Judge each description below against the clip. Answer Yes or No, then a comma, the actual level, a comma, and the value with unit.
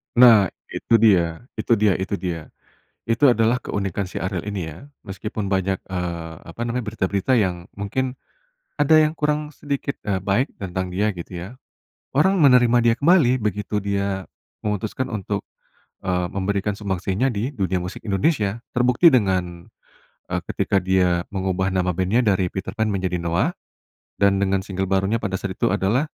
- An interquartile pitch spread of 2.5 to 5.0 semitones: Yes, average, 4.0 semitones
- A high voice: No, low, 100 Hz